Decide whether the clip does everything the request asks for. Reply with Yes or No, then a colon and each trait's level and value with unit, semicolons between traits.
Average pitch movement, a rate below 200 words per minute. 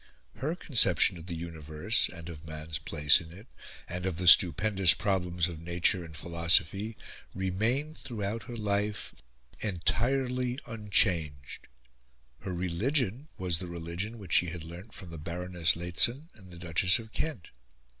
Yes: average, 4.5 semitones; average, 145 wpm